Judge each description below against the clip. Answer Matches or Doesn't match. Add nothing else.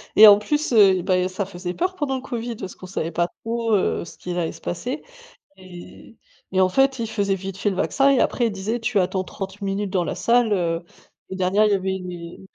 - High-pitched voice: Matches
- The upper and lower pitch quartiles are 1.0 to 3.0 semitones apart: Doesn't match